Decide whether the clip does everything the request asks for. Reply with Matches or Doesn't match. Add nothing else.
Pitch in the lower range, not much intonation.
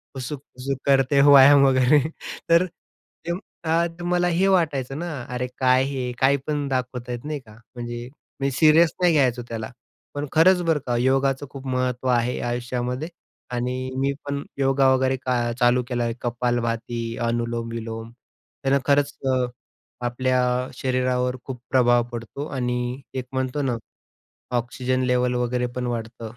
Matches